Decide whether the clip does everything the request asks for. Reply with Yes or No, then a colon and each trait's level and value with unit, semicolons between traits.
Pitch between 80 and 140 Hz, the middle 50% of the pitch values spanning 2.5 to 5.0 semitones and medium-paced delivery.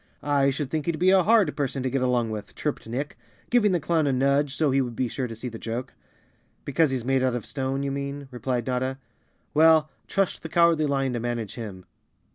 No: low, 135 Hz; average, 3.6 semitones; fast, 220 wpm